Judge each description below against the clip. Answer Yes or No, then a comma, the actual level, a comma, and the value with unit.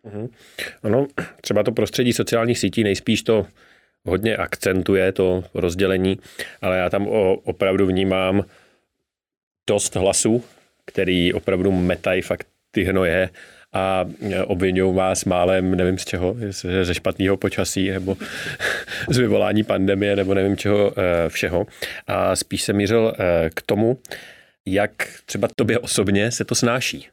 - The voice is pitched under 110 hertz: Yes, very low, 95 Hz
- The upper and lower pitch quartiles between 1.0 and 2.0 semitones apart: Yes, narrow, 1.7 semitones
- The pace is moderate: Yes, average, 130 wpm